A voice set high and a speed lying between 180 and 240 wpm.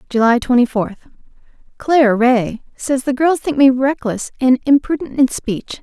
No: very high, 255 Hz; average, 145 wpm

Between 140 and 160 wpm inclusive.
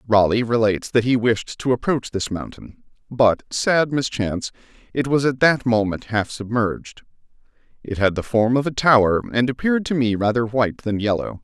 No: average, 180 wpm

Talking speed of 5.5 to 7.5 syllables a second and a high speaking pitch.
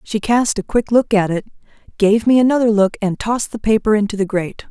Yes: 5.9 syllables/s; high, 215 Hz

